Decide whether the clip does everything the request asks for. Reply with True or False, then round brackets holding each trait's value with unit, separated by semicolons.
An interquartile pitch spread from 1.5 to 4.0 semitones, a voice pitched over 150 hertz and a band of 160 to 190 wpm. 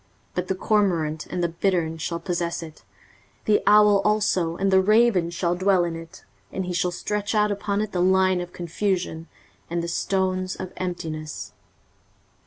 True (2.7 semitones; 185 Hz; 175 wpm)